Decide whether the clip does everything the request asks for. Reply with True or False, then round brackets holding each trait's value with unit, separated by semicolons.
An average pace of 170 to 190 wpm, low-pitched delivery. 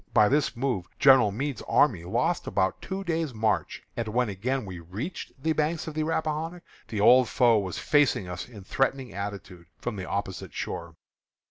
True (175 wpm; 120 Hz)